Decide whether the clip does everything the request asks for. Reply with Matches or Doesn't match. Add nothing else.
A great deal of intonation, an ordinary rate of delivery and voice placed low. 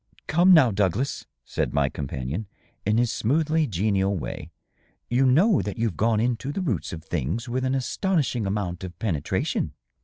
Matches